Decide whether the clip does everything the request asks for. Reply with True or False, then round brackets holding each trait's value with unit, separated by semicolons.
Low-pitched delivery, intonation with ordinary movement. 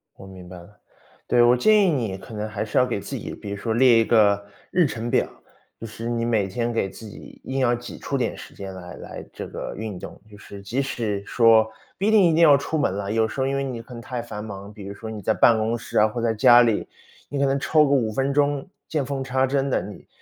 True (115 Hz; 4.2 semitones)